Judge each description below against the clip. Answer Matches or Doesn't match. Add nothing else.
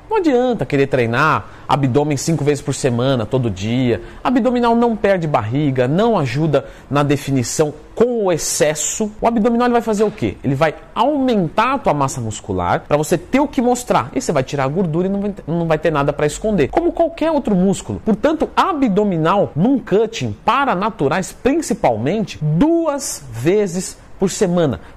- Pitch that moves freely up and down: Matches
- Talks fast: Doesn't match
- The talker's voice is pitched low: Doesn't match